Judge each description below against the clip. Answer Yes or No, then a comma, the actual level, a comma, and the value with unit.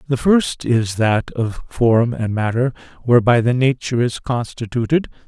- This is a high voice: No, low, 120 Hz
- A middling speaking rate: Yes, average, 150 wpm